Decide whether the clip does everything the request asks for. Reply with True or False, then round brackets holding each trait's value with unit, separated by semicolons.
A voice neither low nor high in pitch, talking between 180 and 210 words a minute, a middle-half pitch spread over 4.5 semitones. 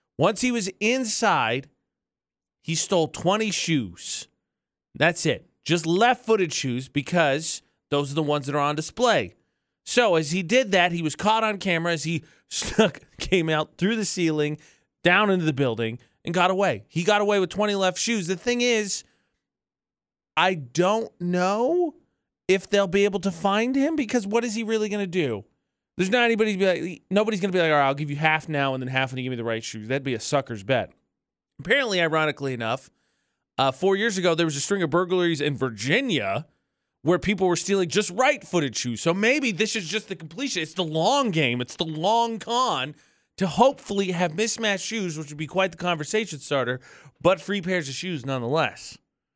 True (180 Hz; 200 wpm; 5.5 semitones)